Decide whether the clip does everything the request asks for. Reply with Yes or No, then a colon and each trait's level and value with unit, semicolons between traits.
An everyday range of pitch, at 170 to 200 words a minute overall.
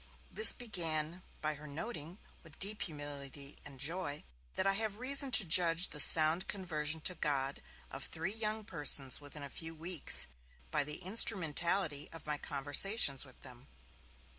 No: average, 4.7 semitones; average, 155 wpm